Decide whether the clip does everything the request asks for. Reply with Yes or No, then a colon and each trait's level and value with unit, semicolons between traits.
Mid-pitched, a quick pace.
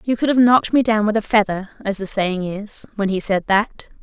No: high, 210 Hz; fast, 255 wpm